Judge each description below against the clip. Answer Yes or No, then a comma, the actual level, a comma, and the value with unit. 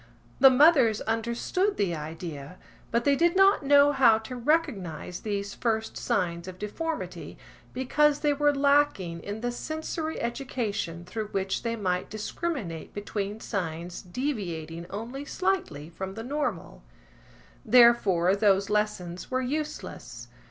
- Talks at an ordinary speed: No, slow, 130 wpm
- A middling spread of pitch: No, wide, 7.4 semitones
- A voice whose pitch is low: No, high, 220 Hz